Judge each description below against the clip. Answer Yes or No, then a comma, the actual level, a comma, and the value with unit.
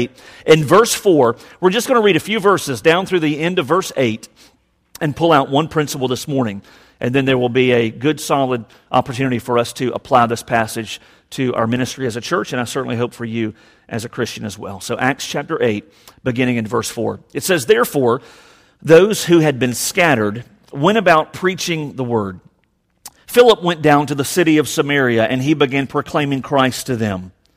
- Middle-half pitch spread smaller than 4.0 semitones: No, average, 4.8 semitones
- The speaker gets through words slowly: No, average, 200 wpm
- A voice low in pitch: Yes, low, 130 Hz